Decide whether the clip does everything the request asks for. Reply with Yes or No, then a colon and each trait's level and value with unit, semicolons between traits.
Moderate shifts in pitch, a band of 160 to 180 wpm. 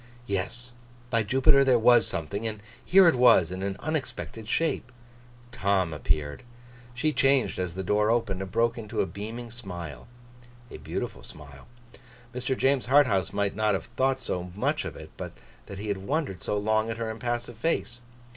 Yes: average, 4.4 semitones; average, 175 wpm